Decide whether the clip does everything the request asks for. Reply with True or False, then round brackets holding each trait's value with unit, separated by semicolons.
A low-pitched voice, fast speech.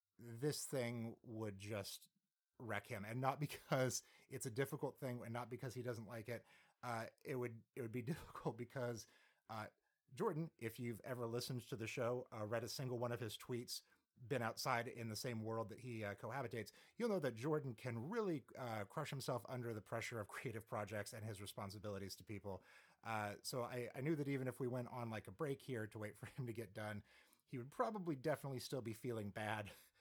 True (120 Hz; 210 wpm)